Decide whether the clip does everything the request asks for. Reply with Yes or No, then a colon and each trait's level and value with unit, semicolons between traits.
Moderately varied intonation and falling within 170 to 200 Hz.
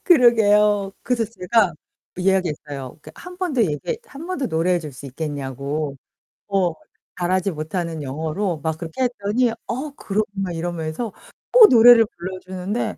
No: wide, 6.4 semitones; medium, 185 Hz